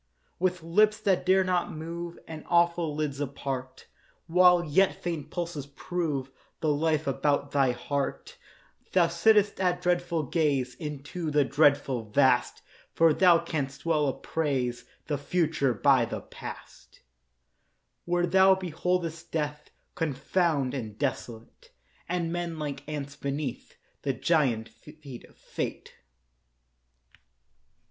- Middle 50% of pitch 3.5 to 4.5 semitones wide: Yes, average, 3.8 semitones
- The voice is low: No, medium, 155 Hz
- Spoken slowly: Yes, slow, 120 wpm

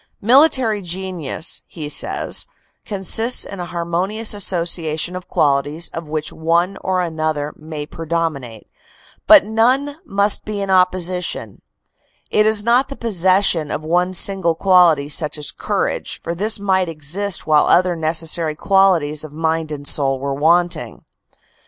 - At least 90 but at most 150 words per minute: Yes, average, 140 wpm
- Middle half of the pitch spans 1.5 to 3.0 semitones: No, average, 3.9 semitones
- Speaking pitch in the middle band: Yes, medium, 175 Hz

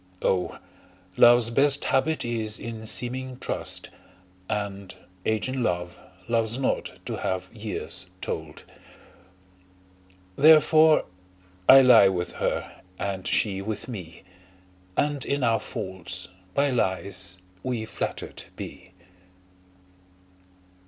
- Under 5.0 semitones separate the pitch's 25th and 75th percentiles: No, wide, 5.4 semitones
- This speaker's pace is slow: Yes, slow, 105 wpm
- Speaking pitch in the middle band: No, low, 110 Hz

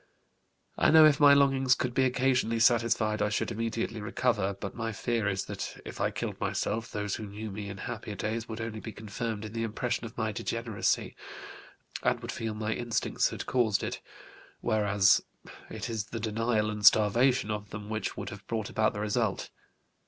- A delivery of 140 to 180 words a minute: No, average, 190 wpm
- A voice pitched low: Yes, low, 110 Hz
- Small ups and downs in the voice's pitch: Yes, narrow, 2.0 semitones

